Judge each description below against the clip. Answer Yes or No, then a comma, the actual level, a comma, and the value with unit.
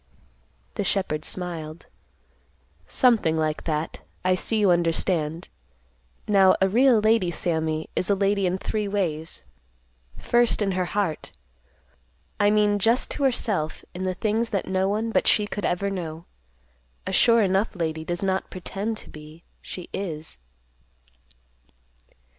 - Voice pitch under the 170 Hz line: No, high, 190 Hz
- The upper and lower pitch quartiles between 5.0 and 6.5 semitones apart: No, average, 3.9 semitones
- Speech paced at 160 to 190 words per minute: No, average, 140 wpm